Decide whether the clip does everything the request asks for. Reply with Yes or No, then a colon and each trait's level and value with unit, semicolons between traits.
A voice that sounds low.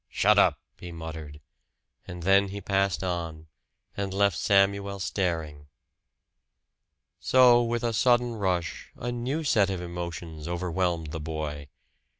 Yes: very low, 95 Hz